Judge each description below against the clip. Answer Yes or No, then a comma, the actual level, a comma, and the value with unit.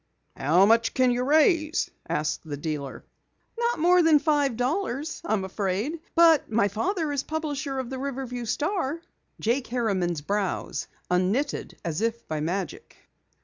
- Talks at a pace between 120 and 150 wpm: Yes, average, 145 wpm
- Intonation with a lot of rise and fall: Yes, wide, 7.7 semitones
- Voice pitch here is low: No, very high, 250 Hz